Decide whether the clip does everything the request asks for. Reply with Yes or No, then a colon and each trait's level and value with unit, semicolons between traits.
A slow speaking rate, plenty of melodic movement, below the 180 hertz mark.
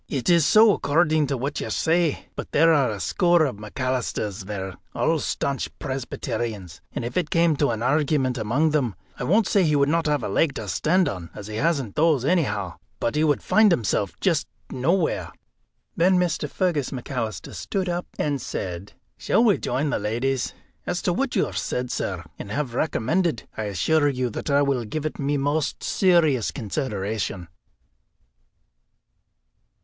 No: average, 175 wpm; wide, 6.0 semitones; medium, 140 Hz